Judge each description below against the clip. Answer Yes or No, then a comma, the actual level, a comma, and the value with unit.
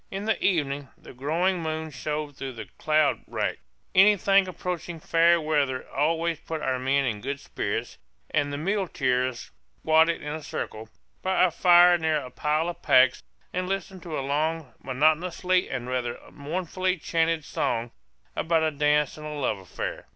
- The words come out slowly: No, average, 165 wpm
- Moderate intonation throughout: Yes, average, 3.9 semitones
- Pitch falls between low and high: Yes, medium, 155 Hz